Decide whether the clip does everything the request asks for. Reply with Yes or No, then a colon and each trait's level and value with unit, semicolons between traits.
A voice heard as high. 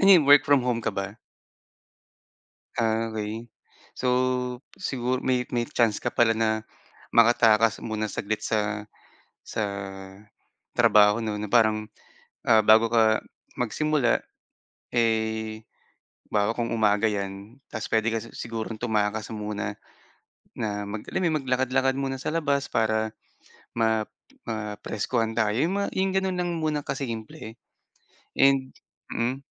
No: low, 115 Hz